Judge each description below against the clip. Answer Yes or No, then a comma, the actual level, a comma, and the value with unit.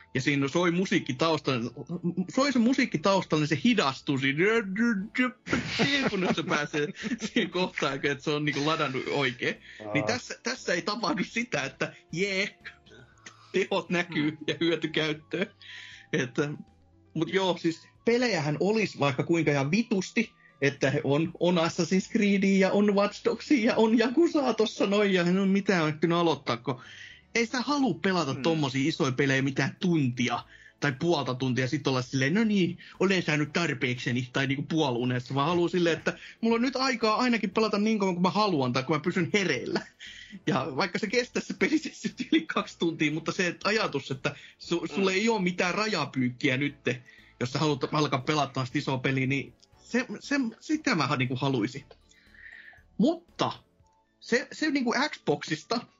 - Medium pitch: Yes, medium, 170 Hz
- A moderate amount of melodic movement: No, wide, 6.8 semitones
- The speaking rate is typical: No, fast, 160 wpm